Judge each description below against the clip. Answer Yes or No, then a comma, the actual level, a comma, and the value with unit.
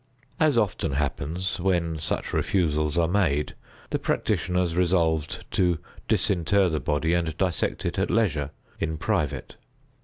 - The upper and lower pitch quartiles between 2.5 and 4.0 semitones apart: Yes, average, 3.2 semitones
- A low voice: Yes, very low, 85 Hz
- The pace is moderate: No, slow, 130 wpm